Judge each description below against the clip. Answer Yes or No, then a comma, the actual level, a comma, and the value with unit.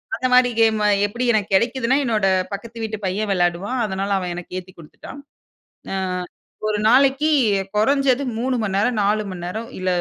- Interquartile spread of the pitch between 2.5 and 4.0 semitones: No, average, 4.5 semitones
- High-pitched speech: Yes, high, 215 Hz